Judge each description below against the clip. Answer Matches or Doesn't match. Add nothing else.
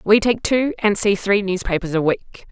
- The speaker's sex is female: Matches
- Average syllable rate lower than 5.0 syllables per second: Matches